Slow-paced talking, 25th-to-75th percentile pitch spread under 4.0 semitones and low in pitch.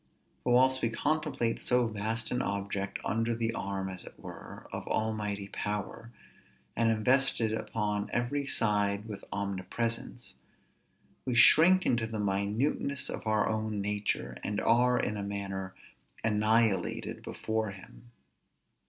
Yes: slow, 130 wpm; average, 2.7 semitones; low, 110 Hz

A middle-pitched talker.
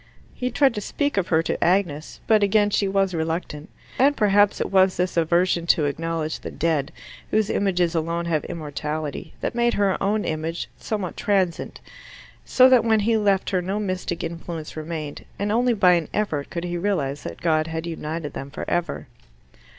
Yes: medium, 175 Hz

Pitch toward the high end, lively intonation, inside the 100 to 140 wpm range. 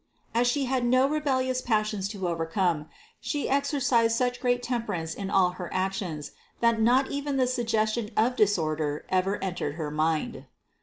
No: high, 220 Hz; wide, 5.9 semitones; average, 160 wpm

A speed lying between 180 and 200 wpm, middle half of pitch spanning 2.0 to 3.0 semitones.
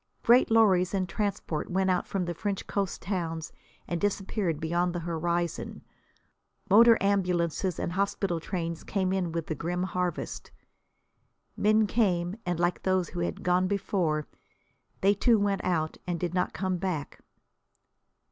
No: average, 145 wpm; narrow, 2.4 semitones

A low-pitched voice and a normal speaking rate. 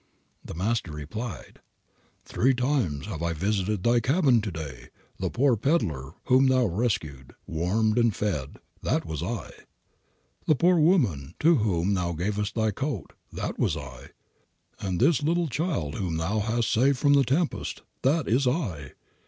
Yes: low, 110 Hz; average, 155 wpm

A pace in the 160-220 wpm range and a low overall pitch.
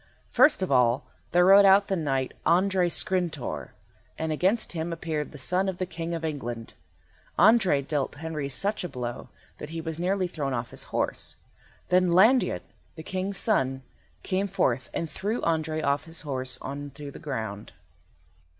No: average, 170 wpm; medium, 160 Hz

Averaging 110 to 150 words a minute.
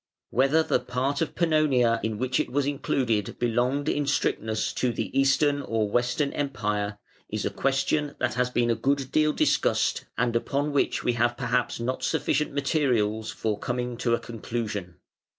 No: average, 170 wpm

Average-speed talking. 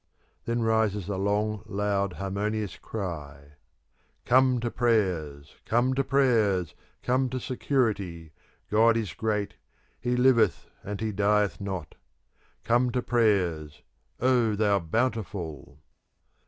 No: slow, 115 wpm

